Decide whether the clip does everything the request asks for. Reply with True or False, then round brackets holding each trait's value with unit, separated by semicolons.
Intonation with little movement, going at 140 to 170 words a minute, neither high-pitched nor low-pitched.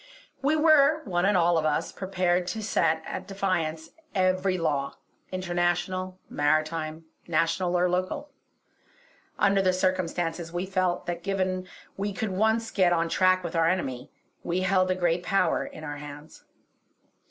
True (2.2 semitones; 150 wpm; 180 Hz)